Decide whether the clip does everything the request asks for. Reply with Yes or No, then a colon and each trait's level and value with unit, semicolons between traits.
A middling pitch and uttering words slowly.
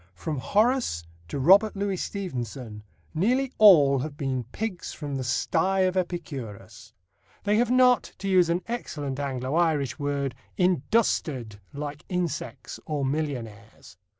Yes: medium, 155 Hz; slow, 130 wpm